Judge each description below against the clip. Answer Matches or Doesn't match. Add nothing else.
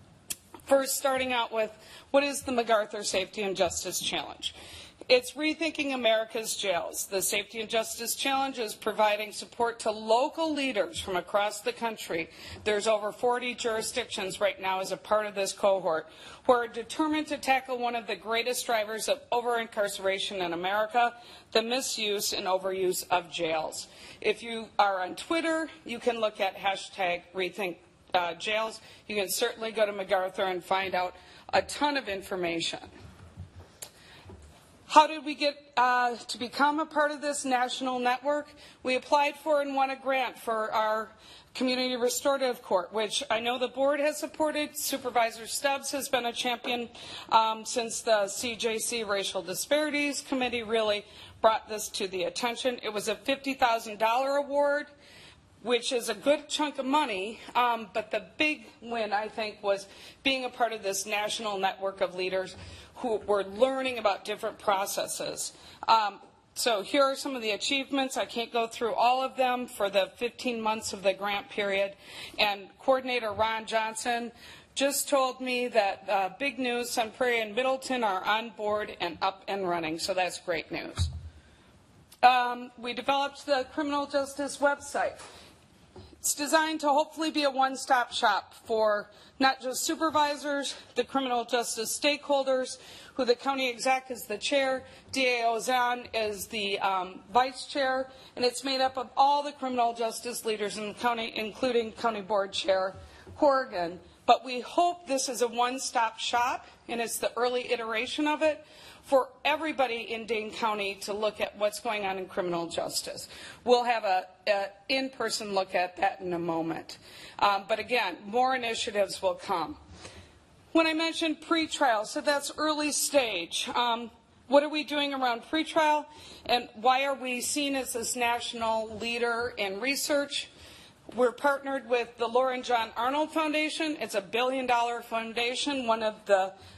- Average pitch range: Matches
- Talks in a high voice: Matches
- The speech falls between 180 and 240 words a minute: Doesn't match